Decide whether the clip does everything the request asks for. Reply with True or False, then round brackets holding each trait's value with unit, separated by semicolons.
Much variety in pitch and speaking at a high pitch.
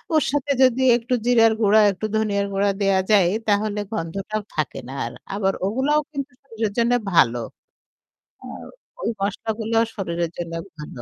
False (3.1 semitones; 210 Hz)